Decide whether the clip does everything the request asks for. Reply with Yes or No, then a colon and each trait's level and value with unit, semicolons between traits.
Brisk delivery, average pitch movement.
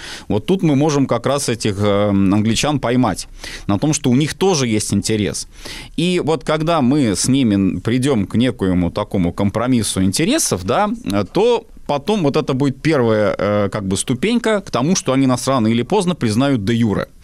No: fast, 175 wpm; wide, 6.7 semitones